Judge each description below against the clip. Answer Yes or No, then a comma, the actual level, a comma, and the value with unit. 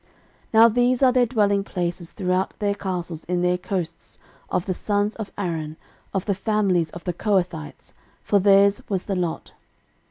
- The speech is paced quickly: No, average, 170 wpm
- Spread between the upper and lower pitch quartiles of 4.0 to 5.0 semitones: No, average, 2.7 semitones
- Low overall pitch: No, high, 195 Hz